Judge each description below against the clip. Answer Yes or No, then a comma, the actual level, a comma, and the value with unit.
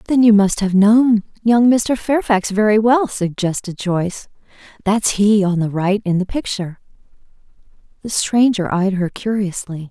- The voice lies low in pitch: No, high, 205 Hz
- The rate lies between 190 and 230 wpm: No, average, 150 wpm